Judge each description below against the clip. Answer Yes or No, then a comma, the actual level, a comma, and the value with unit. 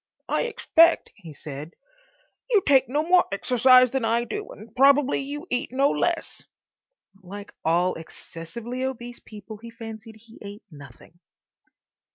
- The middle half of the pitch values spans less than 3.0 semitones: No, average, 5.1 semitones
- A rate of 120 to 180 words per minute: Yes, average, 140 wpm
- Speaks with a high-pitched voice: Yes, high, 230 Hz